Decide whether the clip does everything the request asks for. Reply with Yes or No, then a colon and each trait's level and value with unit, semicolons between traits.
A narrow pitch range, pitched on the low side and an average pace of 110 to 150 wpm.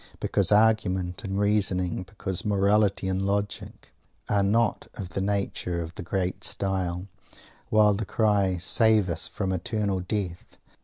Yes: narrow, 2.2 semitones; low, 100 Hz; average, 140 wpm